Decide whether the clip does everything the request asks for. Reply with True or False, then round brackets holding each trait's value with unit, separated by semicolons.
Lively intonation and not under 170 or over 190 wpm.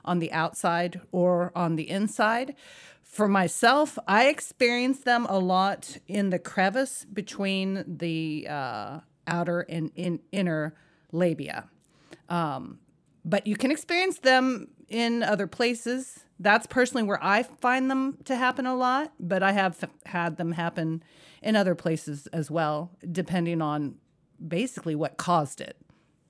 False (5.8 semitones; 140 wpm)